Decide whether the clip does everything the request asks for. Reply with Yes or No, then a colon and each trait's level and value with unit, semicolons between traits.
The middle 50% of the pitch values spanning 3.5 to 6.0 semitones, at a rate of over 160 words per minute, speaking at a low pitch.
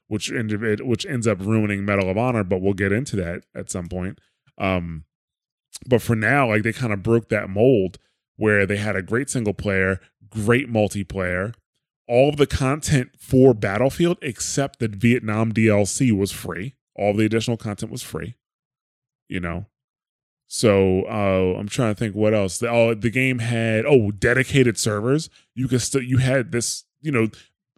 Yes: average, 4.1 semitones; average, 175 wpm; low, 110 Hz